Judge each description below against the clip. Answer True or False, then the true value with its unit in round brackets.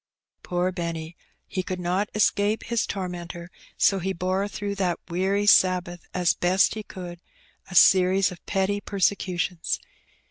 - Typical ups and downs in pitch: False (1.9 semitones)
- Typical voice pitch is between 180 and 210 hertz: True (185 Hz)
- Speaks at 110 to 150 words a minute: True (145 wpm)